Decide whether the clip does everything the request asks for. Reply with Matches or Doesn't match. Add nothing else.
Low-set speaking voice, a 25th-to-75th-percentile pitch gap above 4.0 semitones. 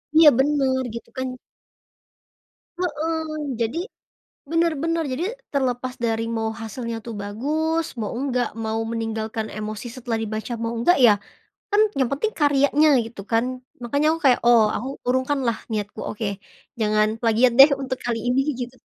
Doesn't match